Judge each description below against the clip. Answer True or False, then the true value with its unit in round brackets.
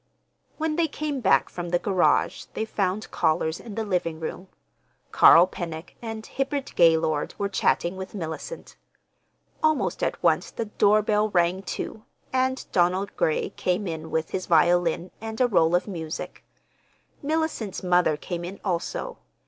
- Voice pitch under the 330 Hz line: True (185 Hz)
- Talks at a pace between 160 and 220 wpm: False (150 wpm)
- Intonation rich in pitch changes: False (4.4 semitones)